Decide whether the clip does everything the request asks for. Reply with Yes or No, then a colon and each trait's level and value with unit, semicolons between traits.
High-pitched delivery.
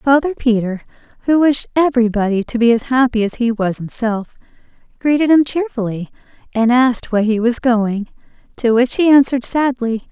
Yes: high, 240 Hz